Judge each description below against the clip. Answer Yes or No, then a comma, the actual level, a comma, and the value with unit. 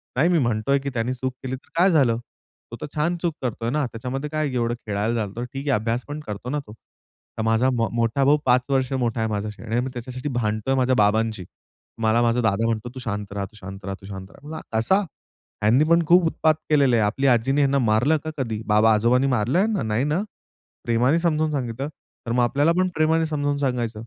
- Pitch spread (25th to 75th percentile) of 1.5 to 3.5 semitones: No, average, 4.2 semitones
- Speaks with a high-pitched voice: No, low, 125 Hz